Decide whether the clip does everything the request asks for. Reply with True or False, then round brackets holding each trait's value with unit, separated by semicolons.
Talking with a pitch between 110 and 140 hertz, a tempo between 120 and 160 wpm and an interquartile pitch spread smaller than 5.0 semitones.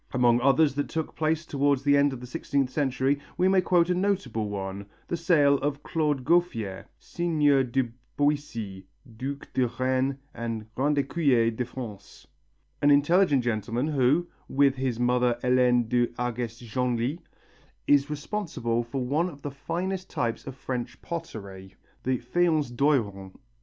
True (135 Hz; 150 wpm; 3.7 semitones)